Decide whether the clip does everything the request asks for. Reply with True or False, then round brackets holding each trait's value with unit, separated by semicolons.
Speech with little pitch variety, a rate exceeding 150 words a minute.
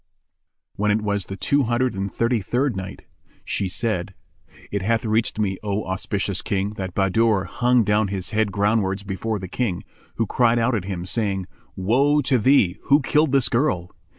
False (3.5 semitones; 180 wpm)